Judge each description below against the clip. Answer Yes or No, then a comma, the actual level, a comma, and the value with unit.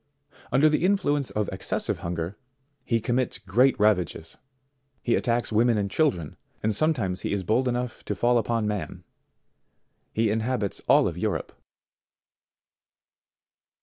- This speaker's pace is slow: Yes, slow, 125 wpm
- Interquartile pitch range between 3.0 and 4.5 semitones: Yes, average, 3.7 semitones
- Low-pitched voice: Yes, low, 115 Hz